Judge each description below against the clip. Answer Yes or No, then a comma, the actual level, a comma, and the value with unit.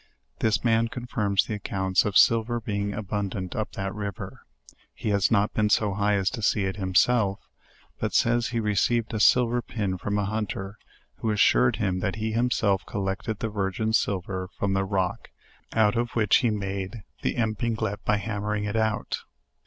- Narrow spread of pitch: Yes, narrow, 2.3 semitones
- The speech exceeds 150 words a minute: Yes, average, 175 wpm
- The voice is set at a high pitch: No, low, 105 Hz